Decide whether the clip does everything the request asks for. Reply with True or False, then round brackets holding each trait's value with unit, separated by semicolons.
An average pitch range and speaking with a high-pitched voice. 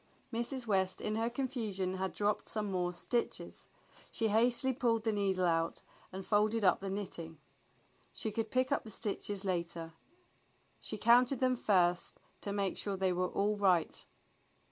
True (3.6 semitones; 205 Hz)